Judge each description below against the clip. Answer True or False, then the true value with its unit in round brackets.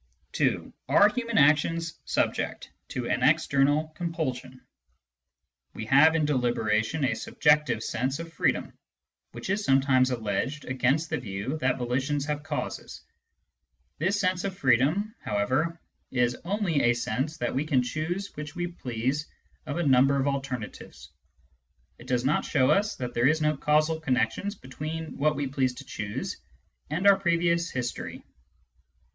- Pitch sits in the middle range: True (145 Hz)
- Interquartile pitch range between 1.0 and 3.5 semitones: False (4.2 semitones)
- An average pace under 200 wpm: True (145 wpm)